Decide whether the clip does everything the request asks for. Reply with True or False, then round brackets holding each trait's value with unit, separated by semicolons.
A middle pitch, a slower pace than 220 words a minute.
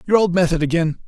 False (175 Hz; 225 wpm)